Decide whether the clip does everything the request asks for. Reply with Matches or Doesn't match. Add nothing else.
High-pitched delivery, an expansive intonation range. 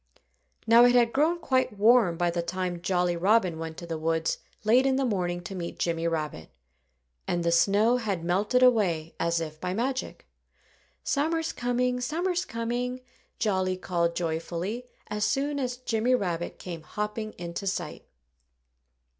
Matches